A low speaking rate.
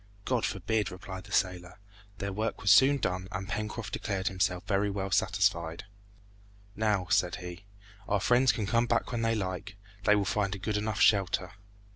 No: average, 175 wpm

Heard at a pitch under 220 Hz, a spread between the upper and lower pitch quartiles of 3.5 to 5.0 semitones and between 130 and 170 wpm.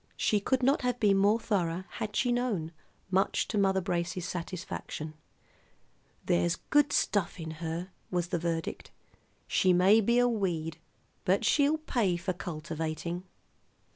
Yes: medium, 185 Hz; average, 4.5 semitones; average, 140 wpm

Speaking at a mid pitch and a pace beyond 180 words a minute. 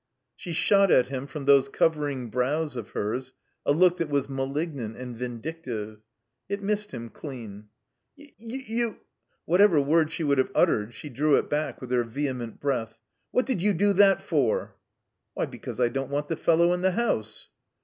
Yes: medium, 145 Hz; average, 190 wpm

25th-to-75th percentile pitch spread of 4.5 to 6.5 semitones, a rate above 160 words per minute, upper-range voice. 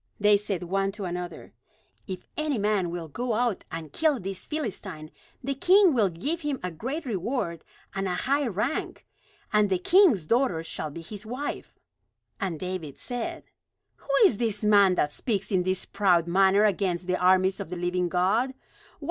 Yes: average, 5.2 semitones; average, 175 wpm; high, 195 Hz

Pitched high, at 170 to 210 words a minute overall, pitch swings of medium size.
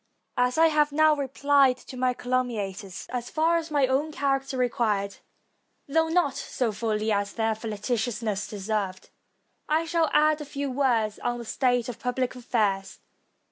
No: very high, 250 Hz; average, 155 wpm; average, 4.6 semitones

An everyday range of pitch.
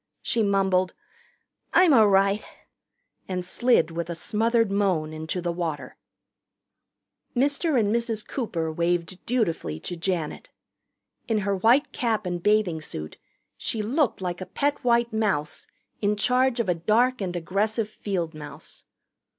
Yes: average, 5.0 semitones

